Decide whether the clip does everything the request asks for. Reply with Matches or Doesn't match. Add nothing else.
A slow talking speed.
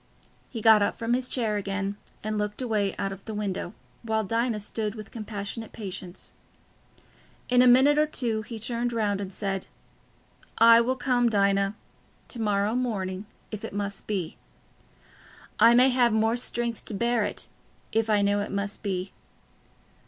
Doesn't match